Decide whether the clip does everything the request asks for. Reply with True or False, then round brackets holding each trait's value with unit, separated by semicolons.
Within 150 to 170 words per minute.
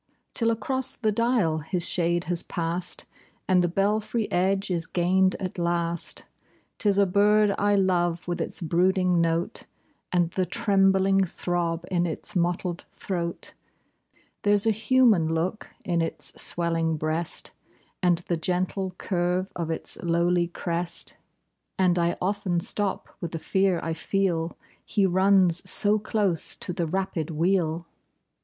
False (140 wpm)